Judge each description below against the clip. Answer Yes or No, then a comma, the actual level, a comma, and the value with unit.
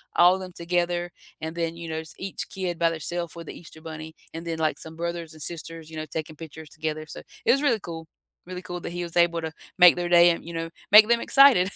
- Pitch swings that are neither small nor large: No, narrow, 1.7 semitones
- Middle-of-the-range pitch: Yes, medium, 170 Hz